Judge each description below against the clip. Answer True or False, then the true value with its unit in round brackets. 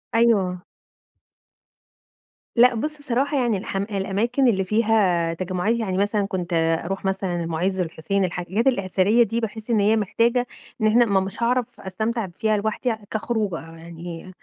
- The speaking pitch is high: True (205 Hz)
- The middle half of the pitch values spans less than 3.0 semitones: False (3.8 semitones)